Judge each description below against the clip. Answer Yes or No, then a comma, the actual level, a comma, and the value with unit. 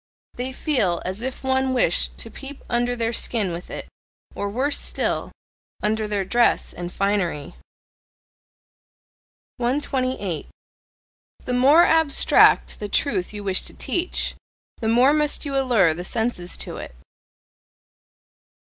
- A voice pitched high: Yes, high, 240 Hz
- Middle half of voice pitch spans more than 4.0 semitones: Yes, average, 5.0 semitones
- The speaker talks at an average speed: No, slow, 130 wpm